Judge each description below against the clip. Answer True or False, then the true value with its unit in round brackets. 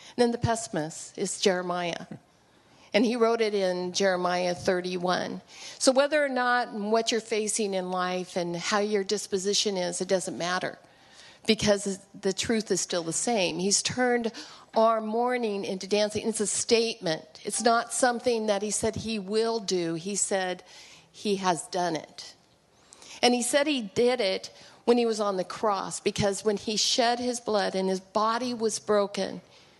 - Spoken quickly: False (165 wpm)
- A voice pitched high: True (205 Hz)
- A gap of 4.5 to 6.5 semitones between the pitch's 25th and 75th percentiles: False (3.7 semitones)